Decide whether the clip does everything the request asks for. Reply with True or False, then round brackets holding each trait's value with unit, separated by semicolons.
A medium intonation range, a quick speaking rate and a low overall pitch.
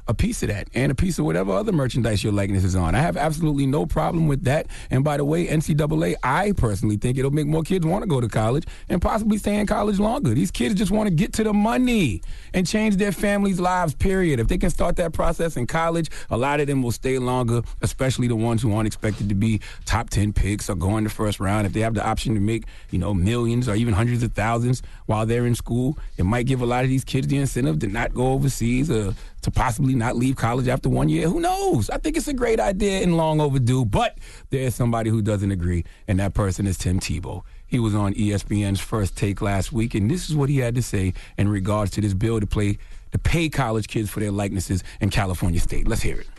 False (6.4 semitones; 250 wpm; 120 Hz)